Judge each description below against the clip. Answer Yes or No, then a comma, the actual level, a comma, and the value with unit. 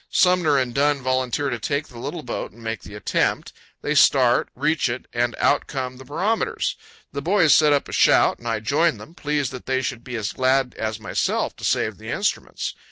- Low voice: Yes, low, 130 Hz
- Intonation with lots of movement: No, average, 3.5 semitones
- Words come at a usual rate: No, fast, 210 wpm